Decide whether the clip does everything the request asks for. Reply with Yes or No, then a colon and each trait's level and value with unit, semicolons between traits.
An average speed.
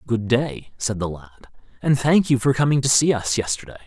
No: fast, 215 wpm